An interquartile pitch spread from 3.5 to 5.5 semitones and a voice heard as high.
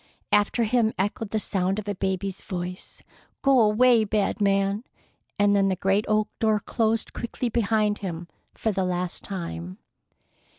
No: narrow, 2.4 semitones; high, 205 Hz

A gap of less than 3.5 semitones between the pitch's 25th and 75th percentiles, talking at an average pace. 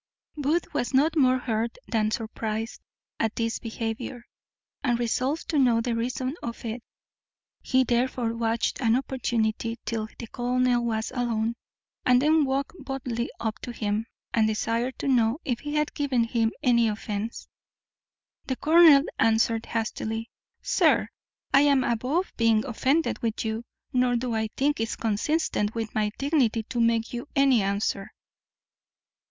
Yes: narrow, 2.6 semitones; average, 145 wpm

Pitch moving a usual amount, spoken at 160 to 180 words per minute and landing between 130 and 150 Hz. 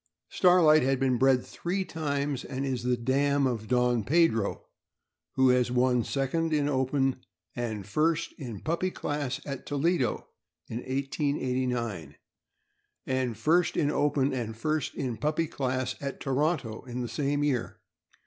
No: average, 3.0 semitones; average, 140 wpm; low, 135 Hz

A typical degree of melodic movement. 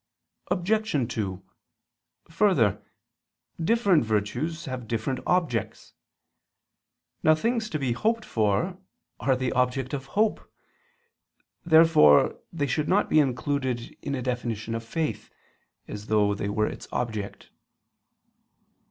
No: wide, 6.5 semitones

